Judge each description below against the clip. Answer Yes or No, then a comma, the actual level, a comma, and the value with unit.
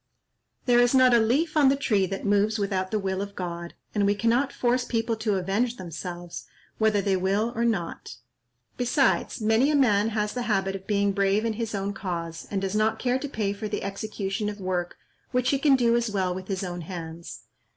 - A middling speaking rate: No, fast, 215 wpm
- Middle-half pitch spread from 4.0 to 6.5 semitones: No, average, 3.6 semitones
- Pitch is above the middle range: Yes, high, 205 Hz